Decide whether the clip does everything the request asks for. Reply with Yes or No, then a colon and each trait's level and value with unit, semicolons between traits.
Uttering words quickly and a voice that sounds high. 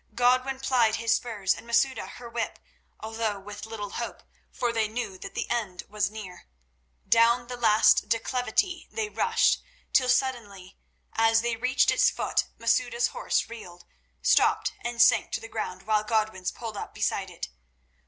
No: average, 160 wpm; high, 225 Hz